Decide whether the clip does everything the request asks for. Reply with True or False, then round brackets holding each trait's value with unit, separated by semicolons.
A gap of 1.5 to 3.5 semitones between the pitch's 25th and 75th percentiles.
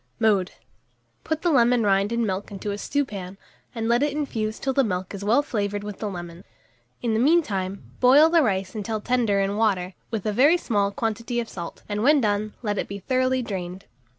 False (3.9 semitones)